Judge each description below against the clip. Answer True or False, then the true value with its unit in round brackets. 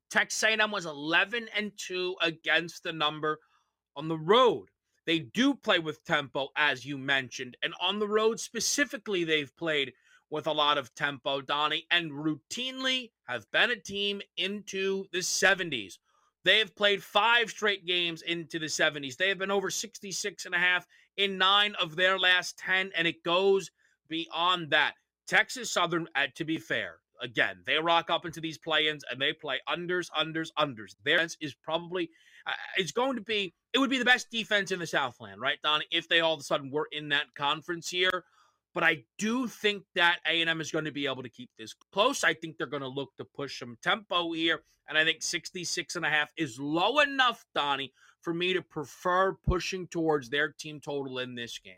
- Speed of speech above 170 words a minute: True (195 wpm)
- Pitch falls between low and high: True (170 Hz)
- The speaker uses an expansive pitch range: False (4.2 semitones)